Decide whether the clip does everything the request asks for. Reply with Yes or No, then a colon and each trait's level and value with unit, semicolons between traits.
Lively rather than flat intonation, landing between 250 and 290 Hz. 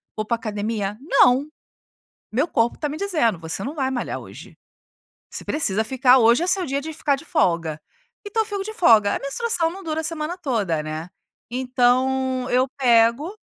Yes: wide, 5.8 semitones; very high, 260 Hz